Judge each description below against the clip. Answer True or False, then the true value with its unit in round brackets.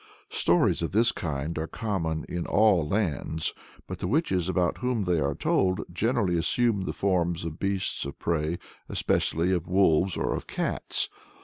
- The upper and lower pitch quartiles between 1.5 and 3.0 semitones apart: False (3.4 semitones)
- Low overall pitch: True (90 Hz)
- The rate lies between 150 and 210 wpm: True (165 wpm)